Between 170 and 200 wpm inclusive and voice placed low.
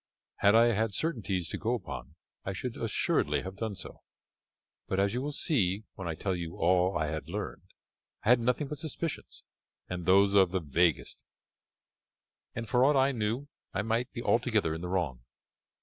Yes: average, 180 wpm; low, 100 Hz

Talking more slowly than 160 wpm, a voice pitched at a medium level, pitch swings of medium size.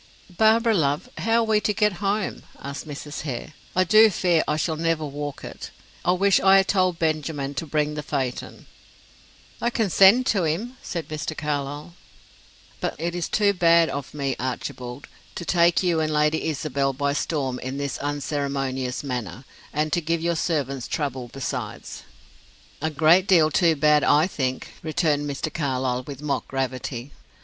No: average, 170 wpm; medium, 155 Hz; average, 3.7 semitones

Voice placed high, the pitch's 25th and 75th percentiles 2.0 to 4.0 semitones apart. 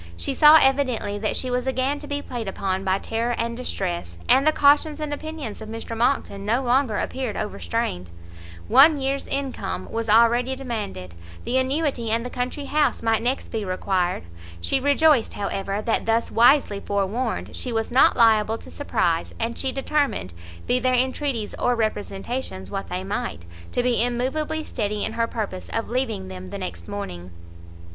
No: high, 235 Hz; average, 4.6 semitones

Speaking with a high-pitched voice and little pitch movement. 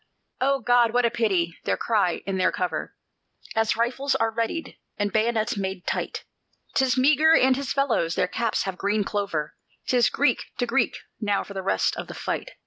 No: high, 225 Hz; average, 4.4 semitones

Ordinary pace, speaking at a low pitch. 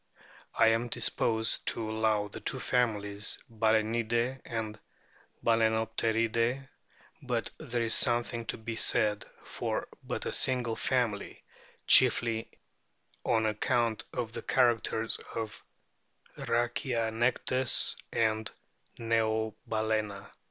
No: slow, 95 wpm; low, 115 Hz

